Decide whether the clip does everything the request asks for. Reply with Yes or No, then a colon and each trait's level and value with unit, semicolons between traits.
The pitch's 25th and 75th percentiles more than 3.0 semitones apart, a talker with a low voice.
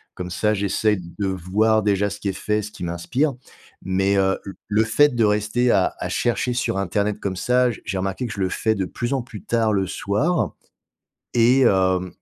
Yes: average, 3.4 semitones; low, 105 Hz